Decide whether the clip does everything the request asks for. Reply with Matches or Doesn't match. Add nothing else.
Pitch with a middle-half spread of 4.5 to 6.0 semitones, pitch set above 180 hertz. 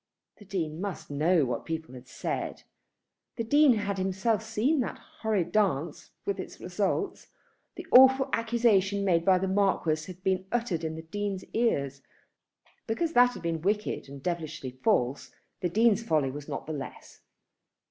Matches